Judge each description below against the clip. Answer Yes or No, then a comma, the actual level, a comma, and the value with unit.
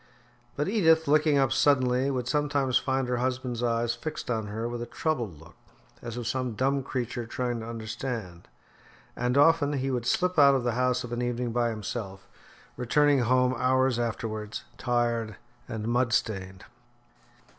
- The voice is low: Yes, low, 125 Hz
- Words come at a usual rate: Yes, average, 165 wpm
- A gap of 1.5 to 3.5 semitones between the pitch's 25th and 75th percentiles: Yes, narrow, 2.5 semitones